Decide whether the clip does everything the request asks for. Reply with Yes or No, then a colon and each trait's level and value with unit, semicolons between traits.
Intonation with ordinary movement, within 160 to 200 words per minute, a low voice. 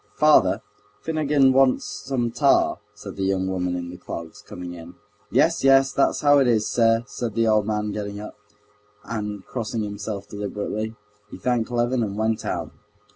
Yes: average, 3.4 semitones; average, 170 wpm; low, 110 Hz